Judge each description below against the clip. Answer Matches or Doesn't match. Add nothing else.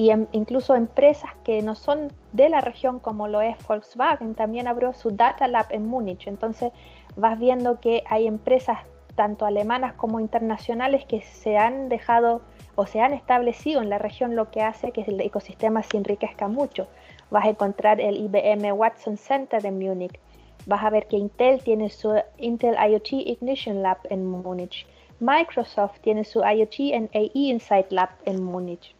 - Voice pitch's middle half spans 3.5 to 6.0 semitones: Doesn't match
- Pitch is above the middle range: Matches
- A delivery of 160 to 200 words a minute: Matches